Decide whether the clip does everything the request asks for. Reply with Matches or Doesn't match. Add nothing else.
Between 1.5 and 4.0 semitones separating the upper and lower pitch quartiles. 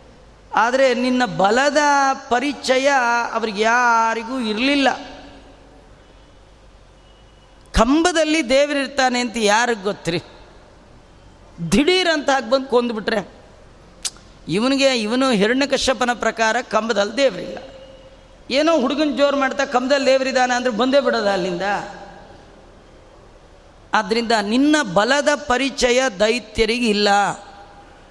Matches